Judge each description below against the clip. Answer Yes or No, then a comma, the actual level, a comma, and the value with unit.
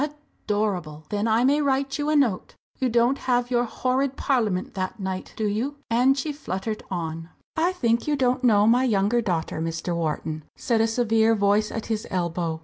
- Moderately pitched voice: No, high, 225 Hz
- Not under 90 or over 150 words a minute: No, average, 185 wpm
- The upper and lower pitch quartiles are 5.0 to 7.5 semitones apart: Yes, wide, 5.4 semitones